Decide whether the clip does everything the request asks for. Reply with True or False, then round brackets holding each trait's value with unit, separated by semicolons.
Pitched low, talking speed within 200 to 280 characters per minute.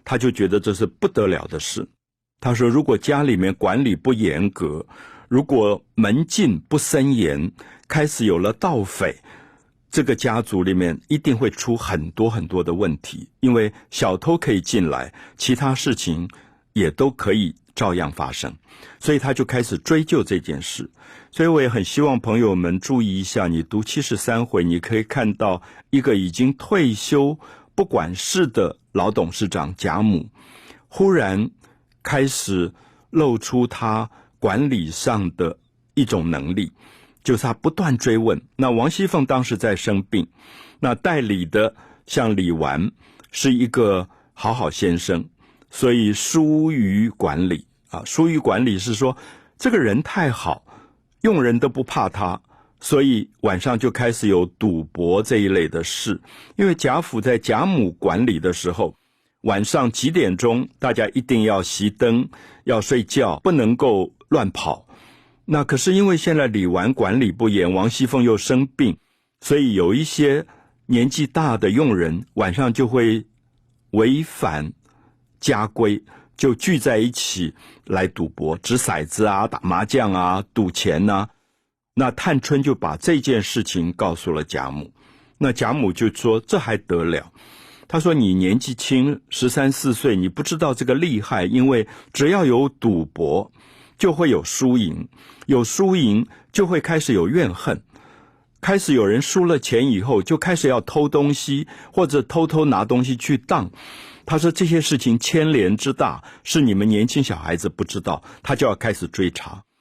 True (120 Hz; 225 characters per minute)